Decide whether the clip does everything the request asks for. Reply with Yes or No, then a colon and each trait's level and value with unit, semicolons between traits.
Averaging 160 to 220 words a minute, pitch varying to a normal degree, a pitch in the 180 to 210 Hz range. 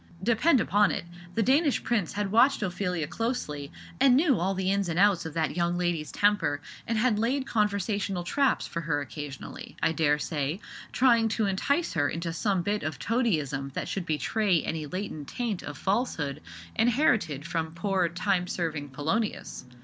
No: average, 170 wpm; wide, 5.8 semitones; high, 190 Hz